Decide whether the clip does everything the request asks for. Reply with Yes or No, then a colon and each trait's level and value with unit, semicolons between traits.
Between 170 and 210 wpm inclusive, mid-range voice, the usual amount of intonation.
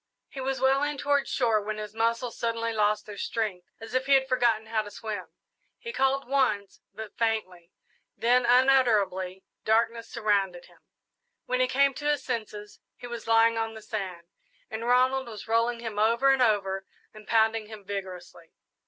No: average, 175 wpm; high, 225 Hz; average, 3.2 semitones